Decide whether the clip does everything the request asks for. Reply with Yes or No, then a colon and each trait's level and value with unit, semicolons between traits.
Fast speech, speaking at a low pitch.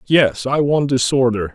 No: average, 155 wpm; low, 130 Hz